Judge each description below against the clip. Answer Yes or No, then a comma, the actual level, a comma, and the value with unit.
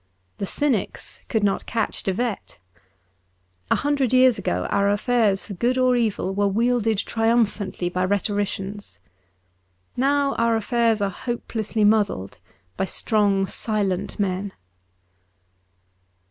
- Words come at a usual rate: No, slow, 120 wpm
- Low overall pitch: No, high, 210 Hz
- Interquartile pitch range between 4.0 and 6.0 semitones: No, average, 3.2 semitones